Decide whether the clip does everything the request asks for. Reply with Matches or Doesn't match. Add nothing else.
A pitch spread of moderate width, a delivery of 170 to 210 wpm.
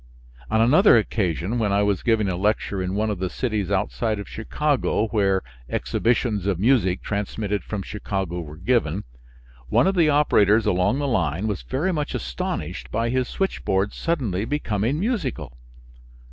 Doesn't match